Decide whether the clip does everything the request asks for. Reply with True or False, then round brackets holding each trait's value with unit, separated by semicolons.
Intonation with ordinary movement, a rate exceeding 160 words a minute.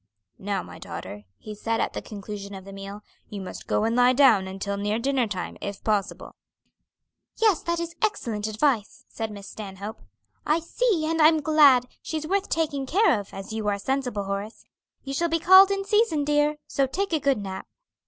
False (7.5 semitones; 195 wpm)